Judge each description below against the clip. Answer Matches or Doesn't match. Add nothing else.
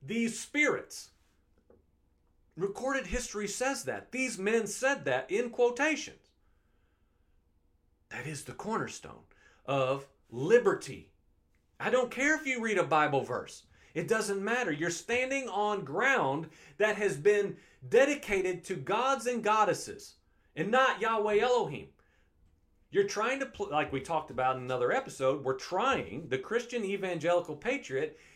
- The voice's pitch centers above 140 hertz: Matches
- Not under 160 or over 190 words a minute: Doesn't match